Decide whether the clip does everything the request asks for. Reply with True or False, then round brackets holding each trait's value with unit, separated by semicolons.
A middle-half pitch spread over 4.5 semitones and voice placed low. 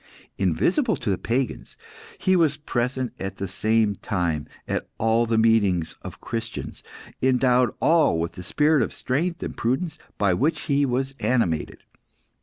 True (5.4 semitones; 120 Hz)